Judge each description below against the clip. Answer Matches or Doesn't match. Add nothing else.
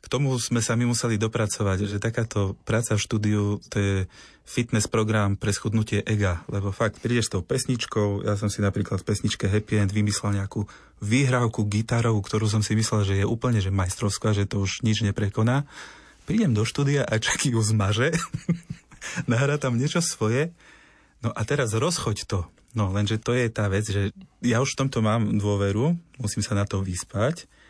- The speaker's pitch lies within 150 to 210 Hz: Doesn't match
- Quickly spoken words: Matches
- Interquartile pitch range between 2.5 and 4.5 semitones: Matches